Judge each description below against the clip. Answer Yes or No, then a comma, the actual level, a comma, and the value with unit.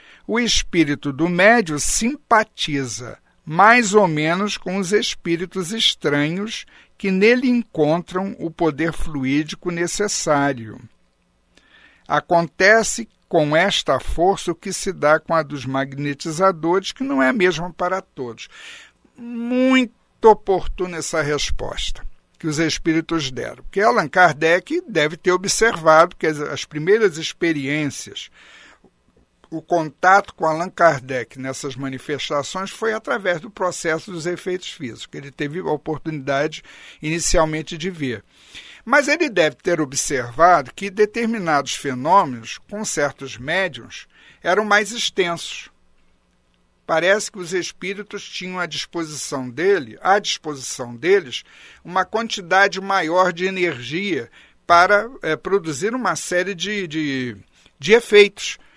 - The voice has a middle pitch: Yes, medium, 170 Hz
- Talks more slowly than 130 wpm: Yes, slow, 120 wpm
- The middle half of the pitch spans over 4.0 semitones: Yes, average, 5.2 semitones